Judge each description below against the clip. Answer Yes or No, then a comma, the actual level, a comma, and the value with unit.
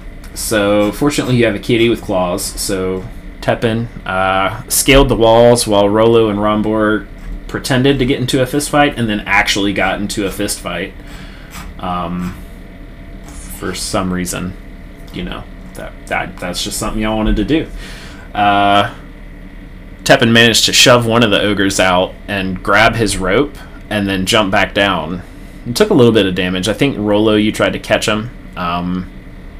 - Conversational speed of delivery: Yes, average, 165 wpm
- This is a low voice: Yes, low, 100 Hz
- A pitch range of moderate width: Yes, average, 3.3 semitones